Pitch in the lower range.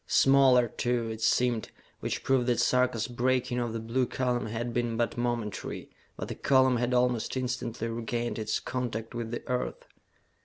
Yes: low, 120 Hz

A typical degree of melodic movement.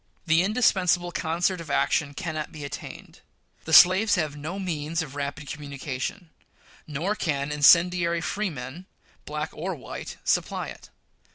Yes: average, 3.6 semitones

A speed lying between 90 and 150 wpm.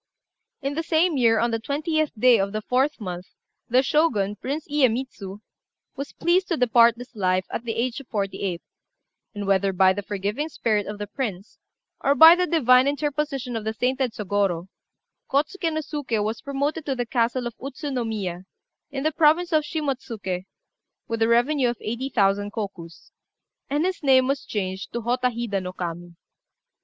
No: average, 180 wpm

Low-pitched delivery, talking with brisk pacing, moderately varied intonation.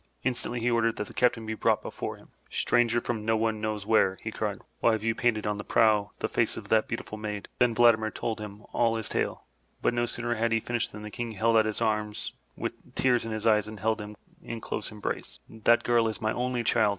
No: low, 110 Hz; fast, 240 wpm; narrow, 1.7 semitones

